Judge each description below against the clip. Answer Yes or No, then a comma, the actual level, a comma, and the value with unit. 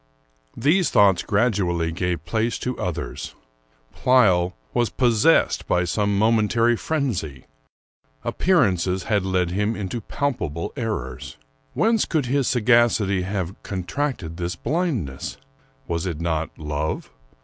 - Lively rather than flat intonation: Yes, wide, 5.7 semitones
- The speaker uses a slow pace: Yes, slow, 115 wpm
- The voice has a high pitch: No, low, 100 Hz